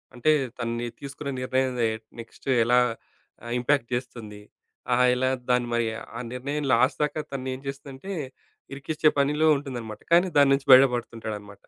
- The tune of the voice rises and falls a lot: No, average, 2.9 semitones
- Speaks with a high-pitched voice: No, low, 130 Hz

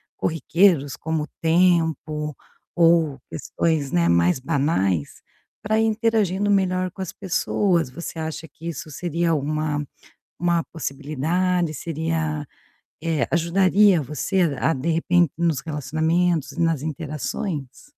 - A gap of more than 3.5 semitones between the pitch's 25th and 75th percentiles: No, average, 2.9 semitones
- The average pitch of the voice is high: No, medium, 165 Hz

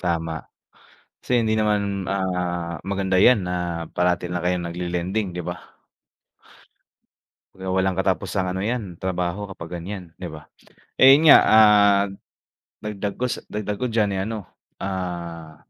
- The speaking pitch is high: No, very low, 95 Hz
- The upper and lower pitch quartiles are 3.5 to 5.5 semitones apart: No, average, 2.8 semitones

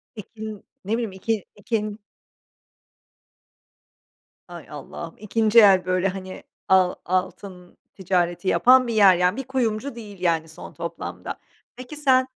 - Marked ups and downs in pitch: No, average, 3.8 semitones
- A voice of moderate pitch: No, high, 200 Hz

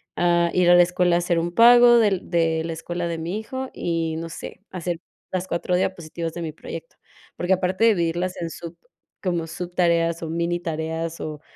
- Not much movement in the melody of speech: Yes, narrow, 1.5 semitones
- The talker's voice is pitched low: No, medium, 175 Hz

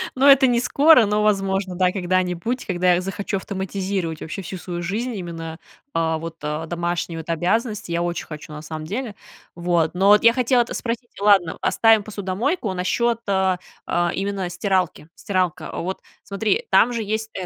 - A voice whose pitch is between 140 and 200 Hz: Yes, high, 190 Hz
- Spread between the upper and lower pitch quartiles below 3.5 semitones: No, average, 3.8 semitones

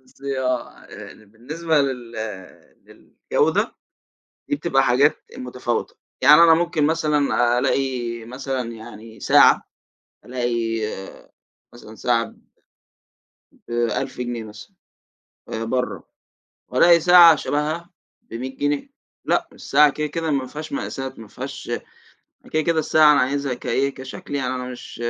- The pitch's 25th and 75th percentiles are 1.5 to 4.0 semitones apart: Yes, average, 3.7 semitones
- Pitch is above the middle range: No, low, 135 Hz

